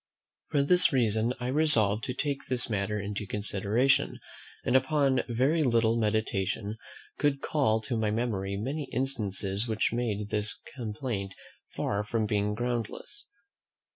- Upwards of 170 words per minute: No, slow, 135 wpm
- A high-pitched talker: No, low, 115 Hz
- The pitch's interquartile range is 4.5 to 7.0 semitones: No, average, 4.0 semitones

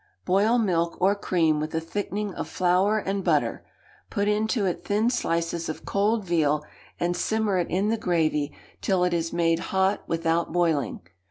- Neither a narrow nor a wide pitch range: Yes, average, 3.6 semitones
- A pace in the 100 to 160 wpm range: No, average, 170 wpm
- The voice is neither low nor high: Yes, medium, 180 Hz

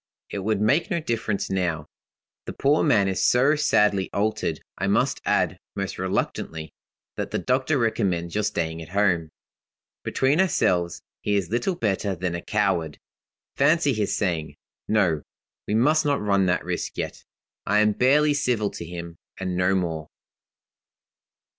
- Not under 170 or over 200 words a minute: No, average, 155 wpm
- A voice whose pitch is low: Yes, low, 100 Hz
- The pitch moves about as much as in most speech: No, wide, 5.8 semitones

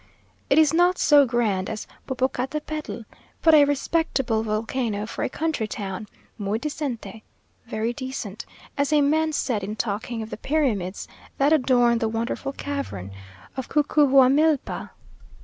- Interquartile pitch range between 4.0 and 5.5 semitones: Yes, average, 5.0 semitones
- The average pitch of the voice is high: Yes, very high, 255 Hz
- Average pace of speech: No, slow, 130 wpm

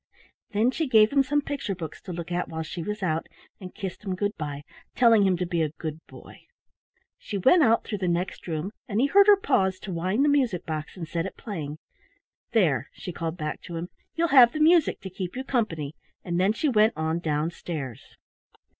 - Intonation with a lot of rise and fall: Yes, wide, 6.1 semitones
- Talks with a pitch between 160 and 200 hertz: Yes, medium, 185 Hz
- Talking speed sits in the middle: No, fast, 215 wpm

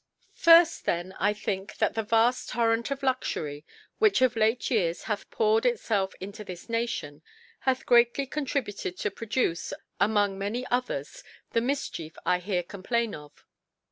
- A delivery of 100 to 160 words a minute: Yes, average, 145 wpm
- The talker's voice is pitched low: No, high, 225 Hz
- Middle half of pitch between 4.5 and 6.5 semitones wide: Yes, average, 4.8 semitones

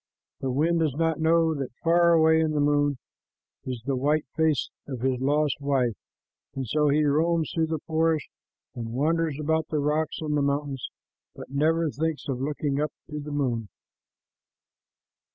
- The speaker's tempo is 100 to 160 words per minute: No, average, 170 wpm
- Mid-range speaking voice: Yes, medium, 150 Hz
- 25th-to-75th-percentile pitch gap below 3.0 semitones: Yes, narrow, 2.4 semitones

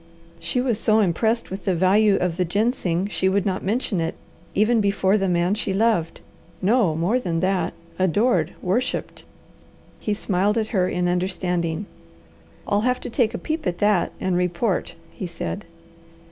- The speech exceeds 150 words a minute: Yes, average, 165 wpm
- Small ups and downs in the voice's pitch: No, average, 3.4 semitones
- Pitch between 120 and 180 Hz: No, high, 195 Hz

